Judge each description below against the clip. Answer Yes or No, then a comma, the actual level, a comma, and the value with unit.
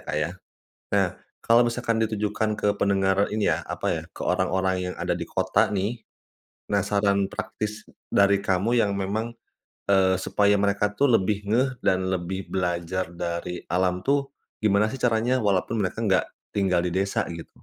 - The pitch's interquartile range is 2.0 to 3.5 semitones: Yes, narrow, 2.5 semitones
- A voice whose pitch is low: Yes, low, 100 Hz